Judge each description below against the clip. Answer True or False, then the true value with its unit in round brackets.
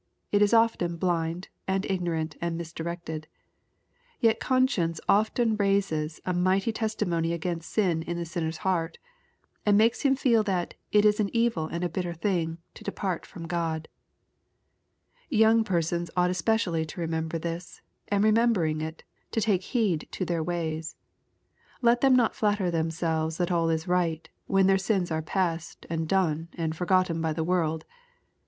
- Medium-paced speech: True (160 wpm)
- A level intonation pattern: False (3.8 semitones)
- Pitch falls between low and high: True (175 Hz)